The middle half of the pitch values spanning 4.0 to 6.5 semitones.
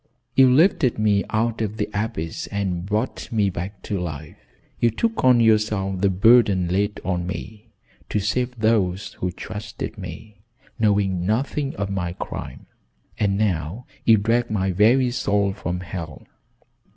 No: average, 3.3 semitones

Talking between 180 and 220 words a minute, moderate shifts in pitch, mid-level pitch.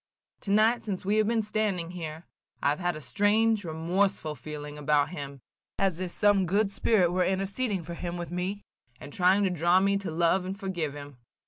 Yes: average, 195 wpm; average, 3.9 semitones; medium, 180 Hz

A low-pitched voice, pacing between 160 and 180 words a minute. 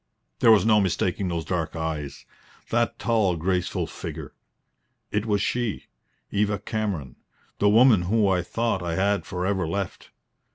No: low, 100 Hz; average, 150 wpm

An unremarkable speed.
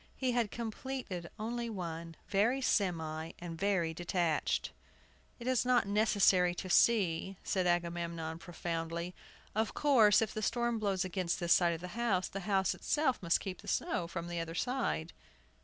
Yes: average, 160 wpm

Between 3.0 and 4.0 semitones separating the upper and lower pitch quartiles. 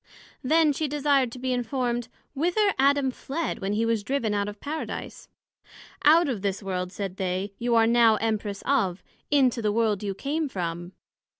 No: wide, 5.6 semitones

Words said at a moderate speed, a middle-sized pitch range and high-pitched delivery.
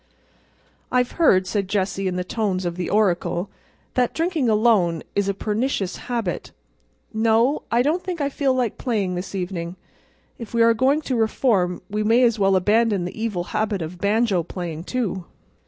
Yes: average, 170 wpm; average, 4.5 semitones; high, 210 Hz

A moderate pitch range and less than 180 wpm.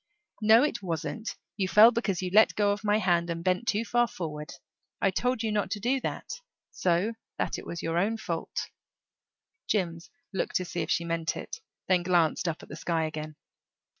No: average, 4.5 semitones; average, 195 wpm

